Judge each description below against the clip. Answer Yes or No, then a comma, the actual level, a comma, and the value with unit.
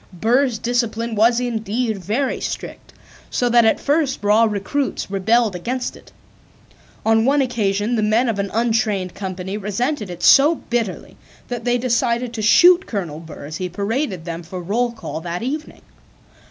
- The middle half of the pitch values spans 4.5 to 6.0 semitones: No, average, 3.7 semitones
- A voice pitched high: Yes, high, 225 Hz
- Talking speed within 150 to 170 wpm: Yes, average, 160 wpm